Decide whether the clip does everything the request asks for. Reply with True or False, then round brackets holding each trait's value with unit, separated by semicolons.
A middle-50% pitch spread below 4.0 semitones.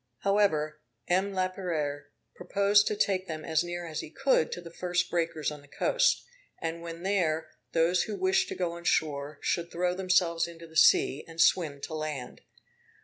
True (2.9 semitones)